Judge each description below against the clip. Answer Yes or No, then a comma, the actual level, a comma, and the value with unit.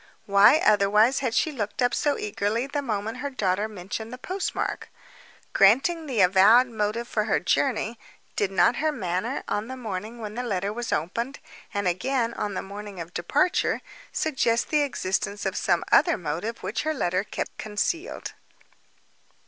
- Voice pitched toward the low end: No, high, 215 Hz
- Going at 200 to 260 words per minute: No, average, 160 wpm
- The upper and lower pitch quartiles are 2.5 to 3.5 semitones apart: No, average, 4.4 semitones